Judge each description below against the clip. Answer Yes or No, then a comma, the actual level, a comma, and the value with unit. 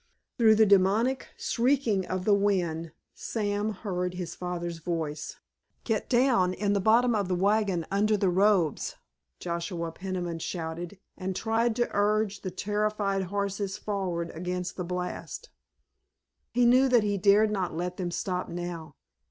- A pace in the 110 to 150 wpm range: Yes, average, 145 wpm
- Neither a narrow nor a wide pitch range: Yes, average, 3.1 semitones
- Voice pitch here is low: No, high, 195 Hz